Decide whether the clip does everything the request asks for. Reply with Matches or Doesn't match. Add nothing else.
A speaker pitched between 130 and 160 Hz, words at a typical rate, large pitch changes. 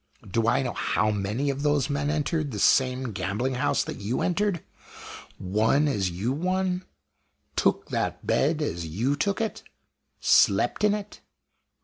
Matches